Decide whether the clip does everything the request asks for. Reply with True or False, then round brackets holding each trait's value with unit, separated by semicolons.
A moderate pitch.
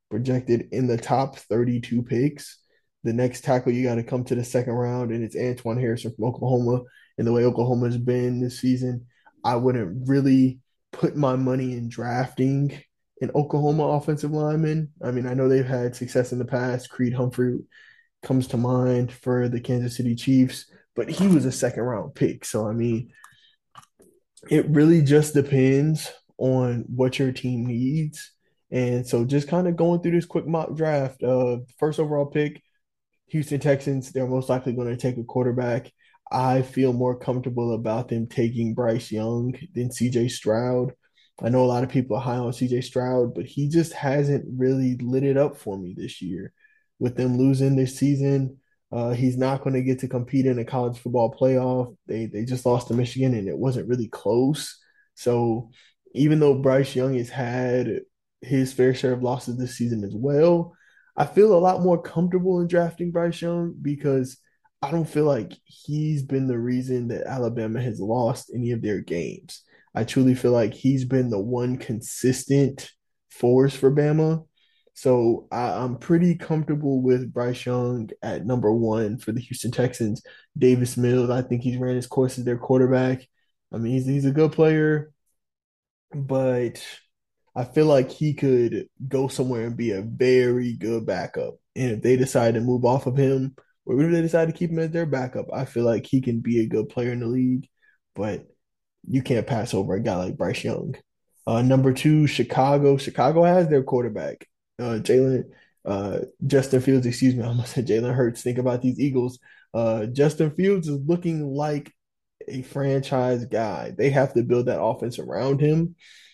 False (130 Hz)